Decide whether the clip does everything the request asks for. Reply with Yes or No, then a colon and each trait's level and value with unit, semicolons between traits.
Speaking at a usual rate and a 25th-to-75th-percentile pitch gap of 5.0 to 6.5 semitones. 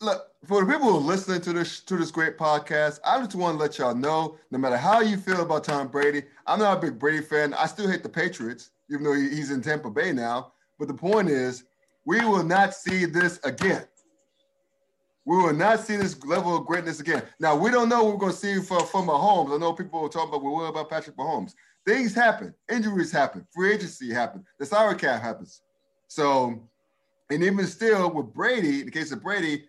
No: fast, 220 wpm; average, 5.3 semitones